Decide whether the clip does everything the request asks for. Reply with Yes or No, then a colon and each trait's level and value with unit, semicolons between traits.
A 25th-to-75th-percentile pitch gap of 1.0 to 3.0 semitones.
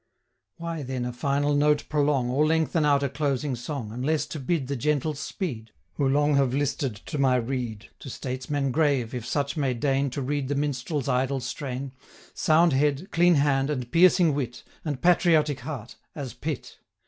Yes: average, 2.7 semitones